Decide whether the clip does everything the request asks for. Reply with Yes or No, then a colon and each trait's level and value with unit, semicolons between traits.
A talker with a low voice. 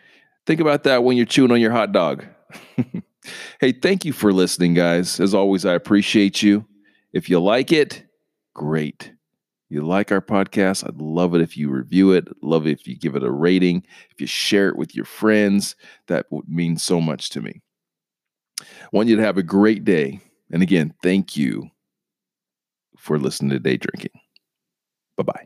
Yes: very low, 95 Hz